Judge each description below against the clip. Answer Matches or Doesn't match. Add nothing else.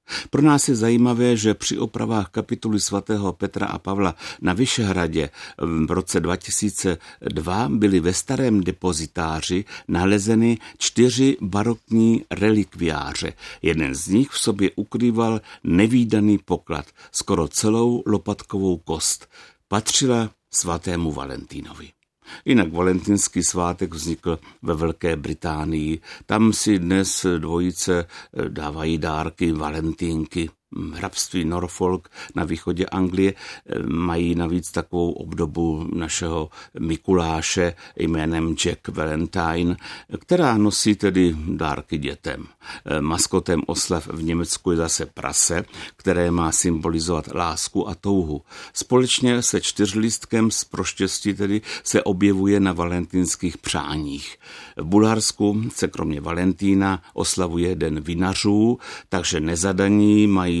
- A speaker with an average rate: Doesn't match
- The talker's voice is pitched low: Matches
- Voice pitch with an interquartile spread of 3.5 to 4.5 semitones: Matches